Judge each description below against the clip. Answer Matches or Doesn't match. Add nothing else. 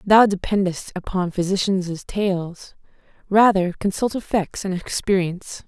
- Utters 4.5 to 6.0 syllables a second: Doesn't match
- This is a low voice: Doesn't match